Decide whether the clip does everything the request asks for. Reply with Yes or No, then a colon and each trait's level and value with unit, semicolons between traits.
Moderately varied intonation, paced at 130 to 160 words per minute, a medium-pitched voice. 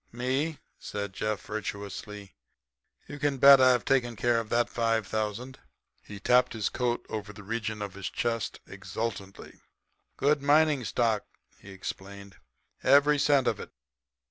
No: average, 4.1 semitones; average, 145 wpm; low, 115 Hz